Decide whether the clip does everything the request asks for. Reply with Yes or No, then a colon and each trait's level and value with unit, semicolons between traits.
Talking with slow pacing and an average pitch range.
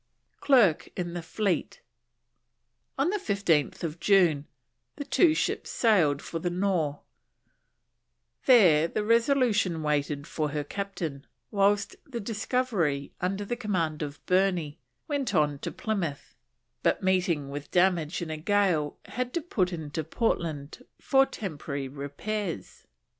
No: slow, 125 wpm; wide, 5.7 semitones